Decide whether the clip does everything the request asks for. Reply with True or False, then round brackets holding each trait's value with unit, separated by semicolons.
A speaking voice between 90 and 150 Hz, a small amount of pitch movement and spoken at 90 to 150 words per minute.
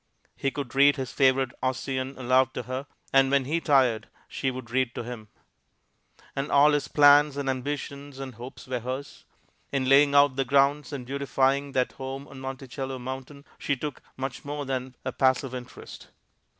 False (135 Hz; 1.5 semitones; 175 wpm)